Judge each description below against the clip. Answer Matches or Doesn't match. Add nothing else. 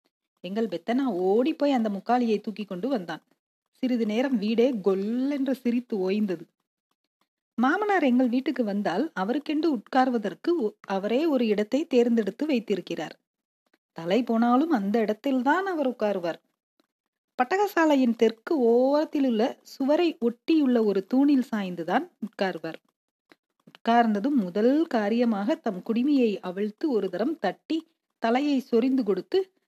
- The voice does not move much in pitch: Doesn't match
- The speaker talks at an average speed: Matches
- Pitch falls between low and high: Doesn't match